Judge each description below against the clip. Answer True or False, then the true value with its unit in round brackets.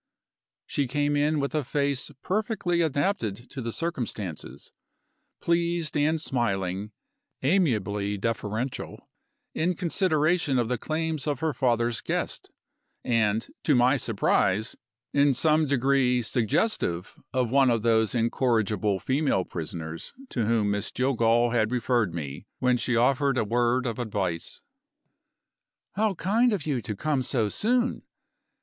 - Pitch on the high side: False (125 Hz)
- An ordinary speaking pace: False (130 wpm)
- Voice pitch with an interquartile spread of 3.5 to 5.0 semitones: False (5.6 semitones)